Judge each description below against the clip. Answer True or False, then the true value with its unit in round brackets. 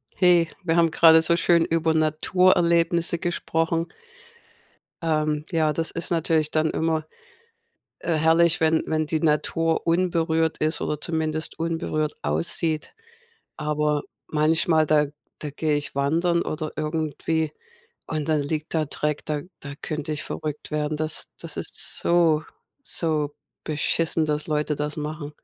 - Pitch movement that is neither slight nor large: False (1.4 semitones)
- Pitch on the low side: False (155 Hz)